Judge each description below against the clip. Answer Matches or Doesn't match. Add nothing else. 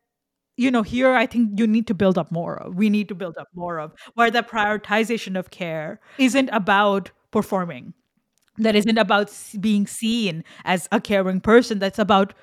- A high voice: Matches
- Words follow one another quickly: Doesn't match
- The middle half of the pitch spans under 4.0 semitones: Matches